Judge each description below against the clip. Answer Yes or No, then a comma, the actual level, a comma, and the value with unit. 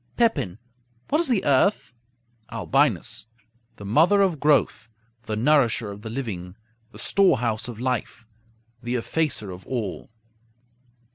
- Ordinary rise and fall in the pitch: No, wide, 6.2 semitones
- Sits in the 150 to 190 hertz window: No, low, 120 Hz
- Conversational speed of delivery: No, slow, 125 wpm